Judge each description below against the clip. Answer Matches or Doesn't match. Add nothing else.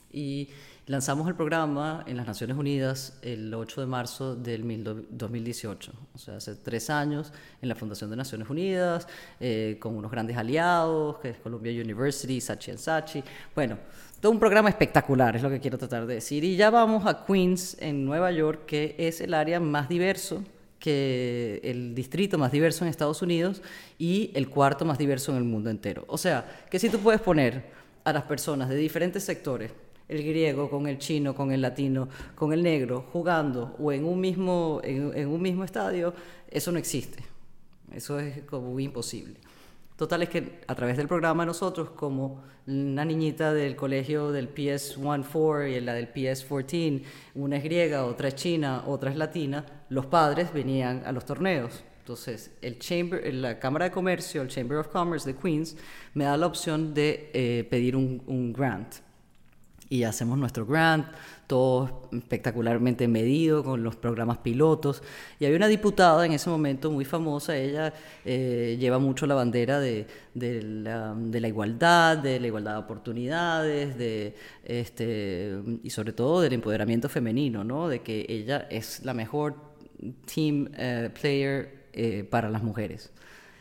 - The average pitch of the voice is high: Doesn't match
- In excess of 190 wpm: Doesn't match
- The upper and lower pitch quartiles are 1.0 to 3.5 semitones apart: Doesn't match